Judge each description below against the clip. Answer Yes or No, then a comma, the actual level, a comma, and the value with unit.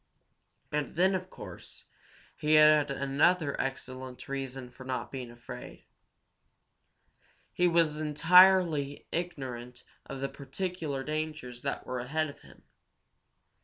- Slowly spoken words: Yes, slow, 115 wpm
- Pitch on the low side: No, medium, 145 Hz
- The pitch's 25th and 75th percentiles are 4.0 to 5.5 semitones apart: No, average, 3.6 semitones